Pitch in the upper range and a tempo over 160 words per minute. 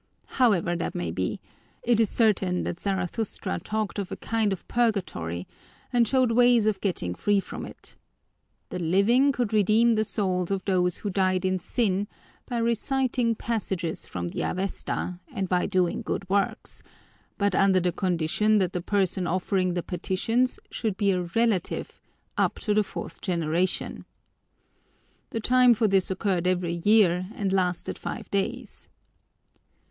No: high, 195 Hz; average, 150 wpm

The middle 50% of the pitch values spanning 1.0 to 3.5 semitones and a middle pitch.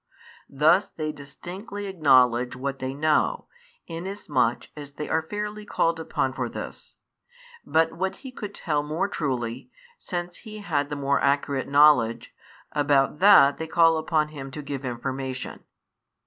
No: average, 4.2 semitones; medium, 150 Hz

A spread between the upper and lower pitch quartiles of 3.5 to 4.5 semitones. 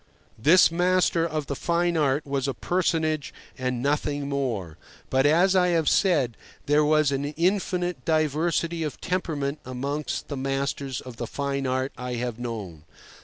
Yes: average, 3.9 semitones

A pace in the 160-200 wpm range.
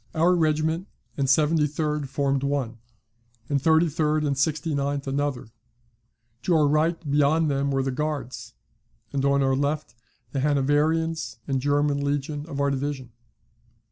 No: slow, 135 wpm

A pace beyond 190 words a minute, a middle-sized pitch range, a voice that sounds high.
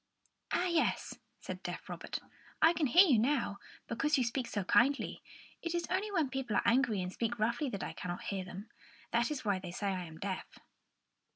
No: average, 200 wpm; wide, 7.1 semitones; high, 235 Hz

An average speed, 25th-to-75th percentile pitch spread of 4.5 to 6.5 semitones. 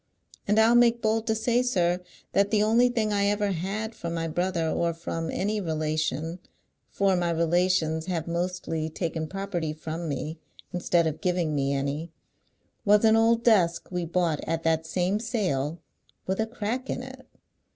Yes: average, 170 wpm; average, 4.8 semitones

